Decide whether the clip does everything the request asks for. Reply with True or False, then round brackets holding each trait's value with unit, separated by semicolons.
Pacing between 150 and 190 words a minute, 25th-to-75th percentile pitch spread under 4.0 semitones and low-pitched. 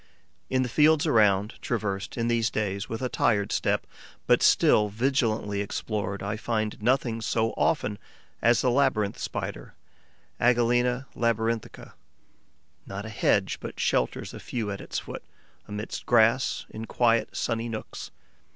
False (140 wpm; 2.5 semitones; 115 Hz)